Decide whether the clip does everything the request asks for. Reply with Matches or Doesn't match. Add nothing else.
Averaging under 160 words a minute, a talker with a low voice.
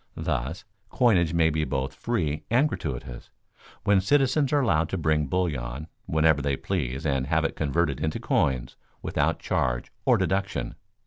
Matches